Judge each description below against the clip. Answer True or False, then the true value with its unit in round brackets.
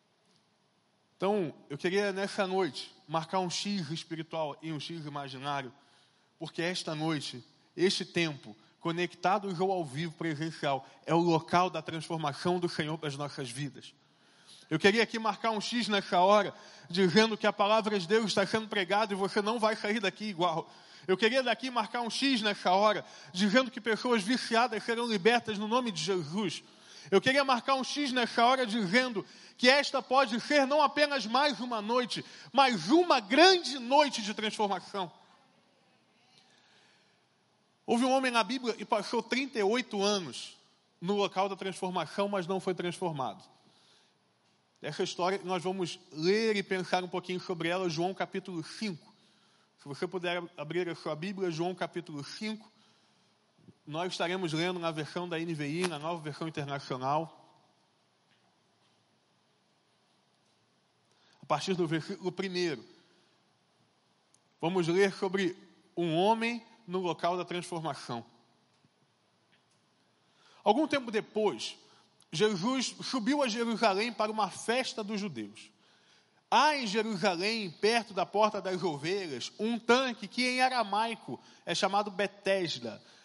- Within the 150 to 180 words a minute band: False (140 wpm)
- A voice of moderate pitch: False (195 Hz)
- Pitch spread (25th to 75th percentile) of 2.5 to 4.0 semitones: False (4.6 semitones)